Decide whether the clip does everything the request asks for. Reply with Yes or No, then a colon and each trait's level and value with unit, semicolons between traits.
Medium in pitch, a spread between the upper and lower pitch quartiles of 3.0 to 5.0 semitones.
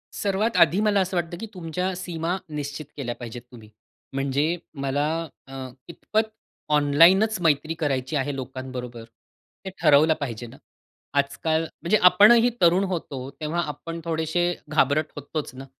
Yes: medium, 155 Hz; average, 4.3 semitones